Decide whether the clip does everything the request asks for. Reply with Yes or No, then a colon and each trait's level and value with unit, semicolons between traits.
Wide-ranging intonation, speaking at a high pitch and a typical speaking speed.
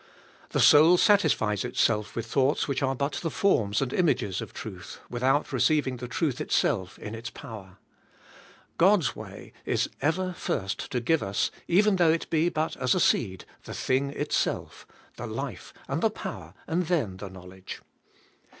No: wide, 7.3 semitones; low, 135 Hz; average, 165 wpm